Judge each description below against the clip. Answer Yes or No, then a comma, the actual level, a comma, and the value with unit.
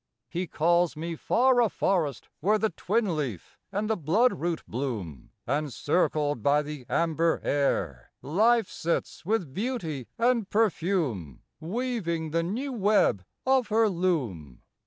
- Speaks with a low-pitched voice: No, medium, 170 Hz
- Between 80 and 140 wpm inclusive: Yes, slow, 135 wpm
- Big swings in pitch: Yes, wide, 6.9 semitones